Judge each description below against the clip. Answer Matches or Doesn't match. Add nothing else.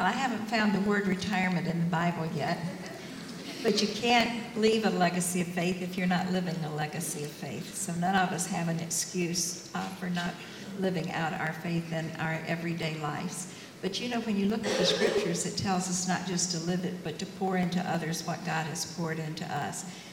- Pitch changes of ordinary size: Doesn't match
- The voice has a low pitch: Doesn't match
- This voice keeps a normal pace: Doesn't match